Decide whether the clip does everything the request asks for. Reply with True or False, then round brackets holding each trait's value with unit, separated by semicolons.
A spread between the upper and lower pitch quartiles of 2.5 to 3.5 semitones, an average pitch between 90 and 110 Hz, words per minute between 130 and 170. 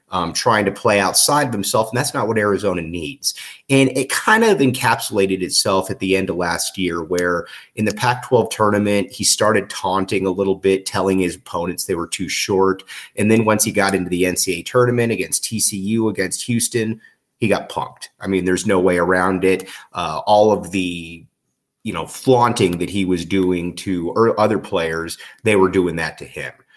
False (3.2 semitones; 95 Hz; 195 wpm)